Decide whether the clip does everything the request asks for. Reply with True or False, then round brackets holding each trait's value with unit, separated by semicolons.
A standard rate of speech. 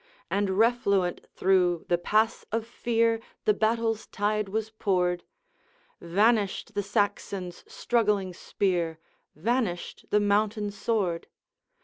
False (105 wpm)